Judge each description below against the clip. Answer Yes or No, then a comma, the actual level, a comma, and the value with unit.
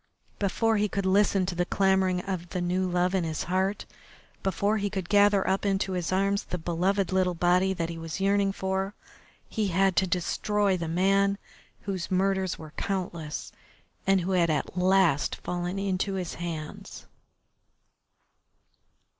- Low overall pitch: No, high, 190 Hz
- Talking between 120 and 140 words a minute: No, average, 155 wpm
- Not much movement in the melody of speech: Yes, narrow, 1.8 semitones